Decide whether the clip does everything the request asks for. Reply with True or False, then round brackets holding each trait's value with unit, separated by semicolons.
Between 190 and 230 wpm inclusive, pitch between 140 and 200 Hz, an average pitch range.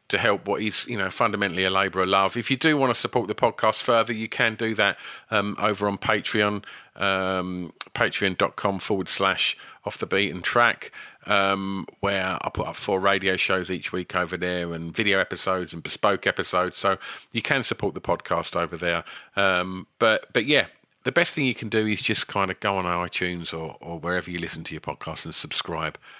False (205 wpm; 95 Hz; 3.1 semitones)